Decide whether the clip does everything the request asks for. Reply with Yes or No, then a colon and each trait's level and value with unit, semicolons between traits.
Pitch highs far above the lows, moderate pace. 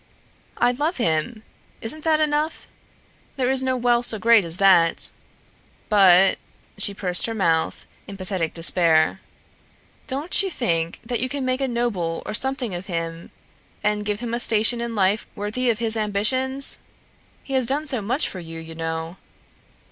Yes: wide, 6.1 semitones; average, 170 wpm